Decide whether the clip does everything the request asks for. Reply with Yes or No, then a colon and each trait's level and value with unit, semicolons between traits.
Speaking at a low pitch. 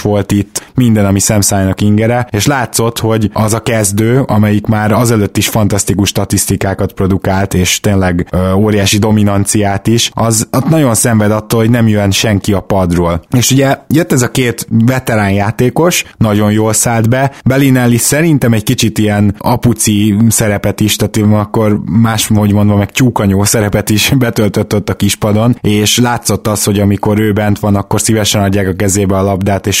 Yes: low, 105 Hz